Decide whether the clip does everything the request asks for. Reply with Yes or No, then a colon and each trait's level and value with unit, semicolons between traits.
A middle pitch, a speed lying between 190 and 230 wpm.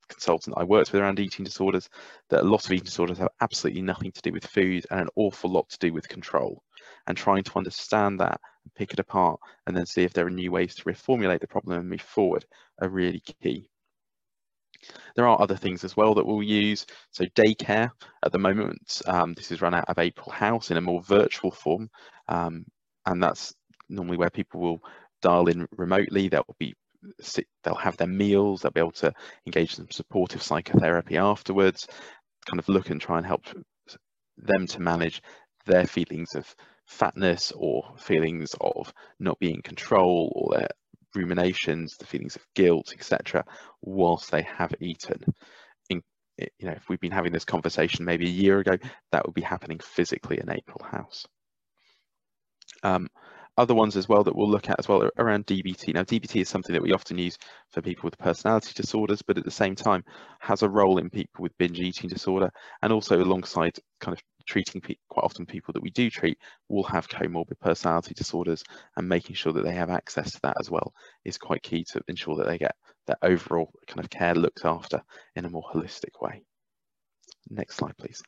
No: very low, 90 Hz; average, 195 wpm